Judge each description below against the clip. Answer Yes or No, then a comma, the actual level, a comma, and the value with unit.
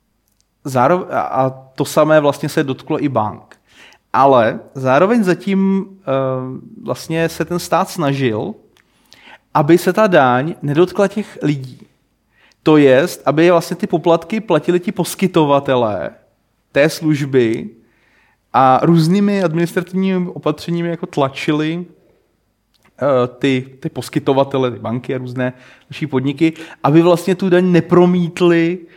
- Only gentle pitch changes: No, average, 4.8 semitones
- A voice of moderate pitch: Yes, medium, 160 Hz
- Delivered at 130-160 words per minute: No, average, 120 wpm